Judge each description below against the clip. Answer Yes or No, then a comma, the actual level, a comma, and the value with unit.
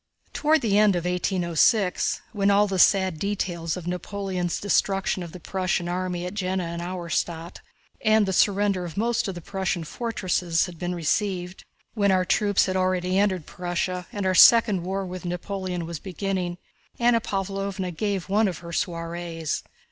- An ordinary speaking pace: Yes, average, 165 wpm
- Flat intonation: Yes, narrow, 2.2 semitones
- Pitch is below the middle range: No, medium, 185 Hz